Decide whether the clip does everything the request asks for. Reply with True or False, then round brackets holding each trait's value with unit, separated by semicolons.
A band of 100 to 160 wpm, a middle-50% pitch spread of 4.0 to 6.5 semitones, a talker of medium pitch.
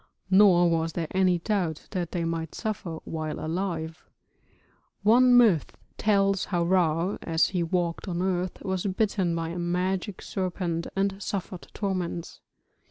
False (140 wpm; 2.6 semitones; 180 Hz)